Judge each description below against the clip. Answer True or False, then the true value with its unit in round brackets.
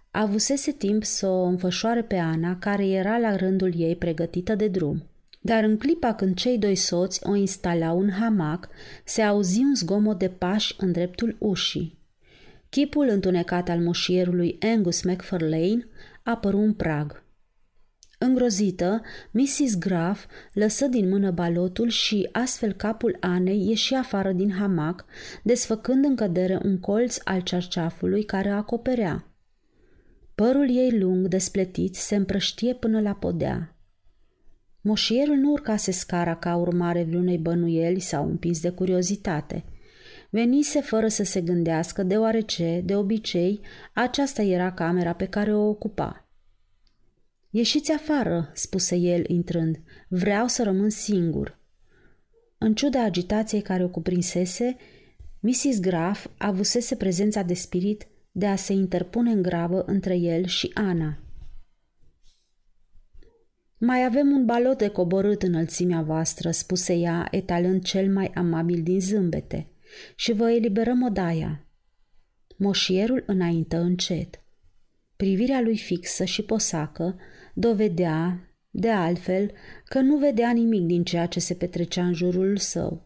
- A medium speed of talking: True (130 wpm)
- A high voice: True (195 Hz)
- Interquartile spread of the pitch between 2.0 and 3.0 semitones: False (4.0 semitones)